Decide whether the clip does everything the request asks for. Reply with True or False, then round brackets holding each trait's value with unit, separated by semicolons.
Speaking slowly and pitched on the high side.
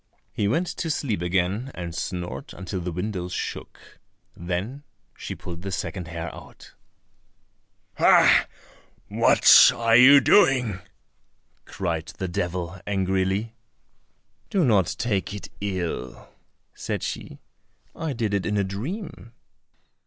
False (120 wpm; 95 Hz)